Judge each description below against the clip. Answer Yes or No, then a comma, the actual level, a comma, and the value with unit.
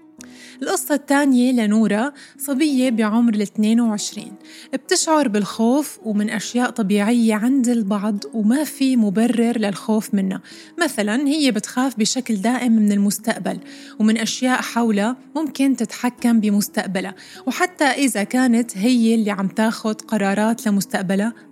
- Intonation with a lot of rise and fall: No, average, 3.6 semitones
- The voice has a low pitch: No, high, 230 Hz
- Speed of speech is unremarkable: Yes, average, 110 wpm